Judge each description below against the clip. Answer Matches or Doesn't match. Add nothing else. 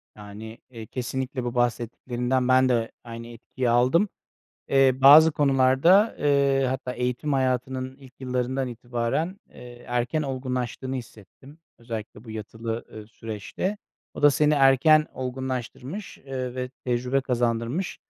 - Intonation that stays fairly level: Matches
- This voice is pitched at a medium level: Doesn't match